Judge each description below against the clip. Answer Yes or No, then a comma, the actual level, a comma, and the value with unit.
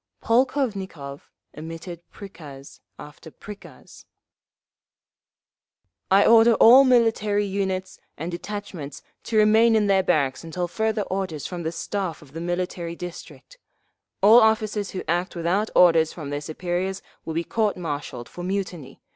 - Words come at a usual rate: No, slow, 130 wpm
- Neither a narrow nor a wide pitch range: Yes, average, 4.2 semitones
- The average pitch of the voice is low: No, medium, 185 Hz